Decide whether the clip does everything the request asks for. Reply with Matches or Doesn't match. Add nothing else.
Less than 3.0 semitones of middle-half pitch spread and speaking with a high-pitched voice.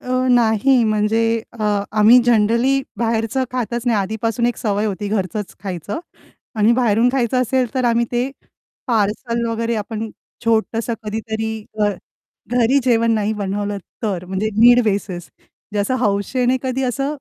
Matches